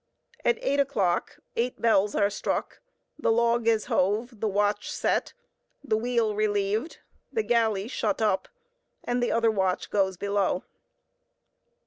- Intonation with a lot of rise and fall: No, average, 2.7 semitones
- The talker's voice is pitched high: Yes, high, 215 Hz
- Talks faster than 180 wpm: No, slow, 135 wpm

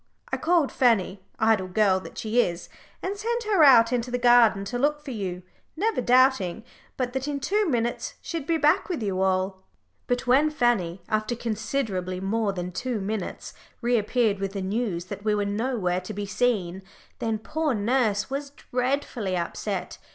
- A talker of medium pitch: No, high, 230 Hz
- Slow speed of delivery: No, average, 175 wpm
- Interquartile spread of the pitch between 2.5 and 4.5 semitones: No, average, 5.2 semitones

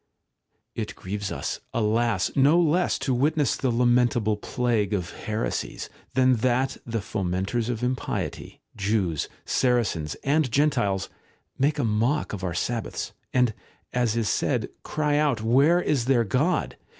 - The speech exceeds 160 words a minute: No, average, 155 wpm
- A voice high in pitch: No, low, 120 Hz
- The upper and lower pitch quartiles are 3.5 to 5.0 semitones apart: Yes, average, 4.1 semitones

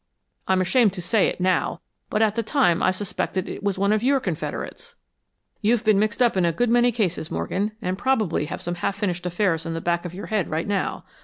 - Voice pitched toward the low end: No, high, 195 Hz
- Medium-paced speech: No, fast, 230 wpm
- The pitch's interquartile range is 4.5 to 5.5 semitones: No, average, 3.8 semitones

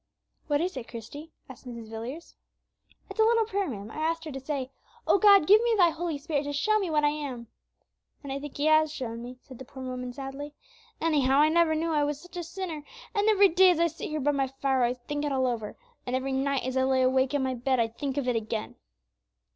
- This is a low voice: No, very high, 285 Hz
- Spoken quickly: Yes, fast, 250 wpm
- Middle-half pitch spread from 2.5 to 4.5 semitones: Yes, average, 3.9 semitones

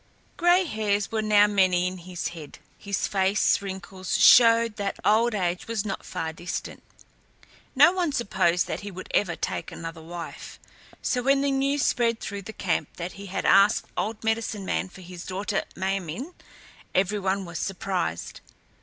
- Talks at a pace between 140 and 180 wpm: Yes, average, 170 wpm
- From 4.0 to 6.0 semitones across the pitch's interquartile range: No, average, 3.4 semitones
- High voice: Yes, high, 200 Hz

